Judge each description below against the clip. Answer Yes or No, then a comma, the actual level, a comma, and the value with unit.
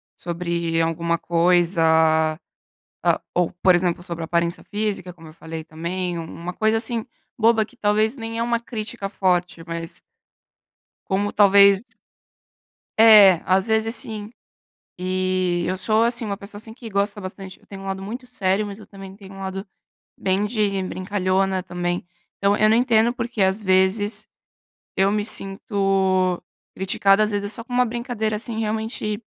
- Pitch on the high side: Yes, high, 195 Hz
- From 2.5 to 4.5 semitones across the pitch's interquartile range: Yes, average, 3.2 semitones